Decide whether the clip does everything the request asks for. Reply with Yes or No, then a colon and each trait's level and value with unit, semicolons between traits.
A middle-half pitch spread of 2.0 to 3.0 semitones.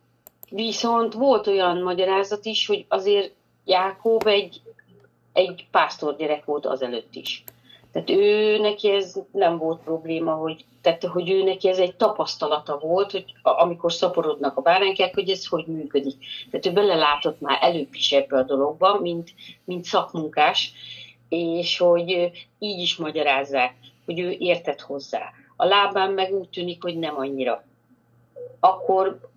No: average, 4.3 semitones